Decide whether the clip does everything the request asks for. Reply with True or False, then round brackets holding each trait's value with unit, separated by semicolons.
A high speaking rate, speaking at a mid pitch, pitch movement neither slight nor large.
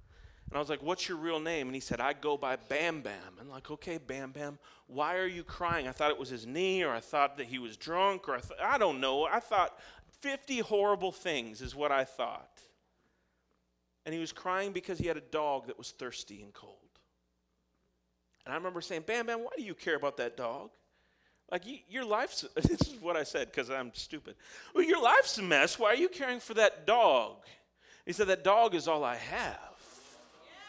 False (220 wpm; 155 Hz; 6.6 semitones)